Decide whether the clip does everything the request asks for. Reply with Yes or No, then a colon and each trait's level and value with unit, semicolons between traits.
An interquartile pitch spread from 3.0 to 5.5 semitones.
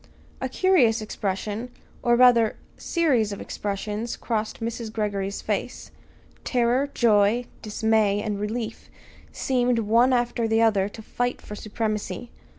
No: narrow, 2.6 semitones